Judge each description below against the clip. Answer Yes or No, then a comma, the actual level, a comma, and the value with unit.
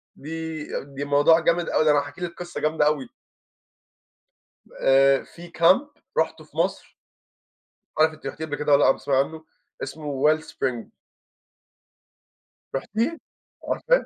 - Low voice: No, medium, 155 Hz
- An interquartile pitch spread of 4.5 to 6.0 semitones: No, average, 2.7 semitones